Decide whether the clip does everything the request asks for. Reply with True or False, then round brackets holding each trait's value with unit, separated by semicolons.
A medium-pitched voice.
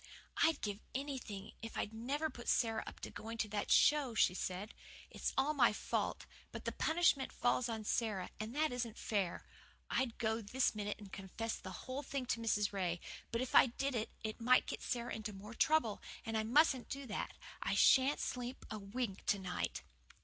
False (230 Hz)